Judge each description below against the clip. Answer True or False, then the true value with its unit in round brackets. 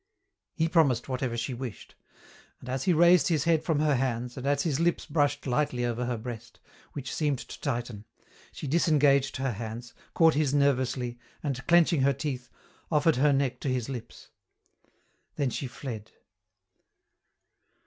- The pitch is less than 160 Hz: True (135 Hz)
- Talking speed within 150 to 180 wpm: True (160 wpm)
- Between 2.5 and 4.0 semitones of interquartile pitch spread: True (3.3 semitones)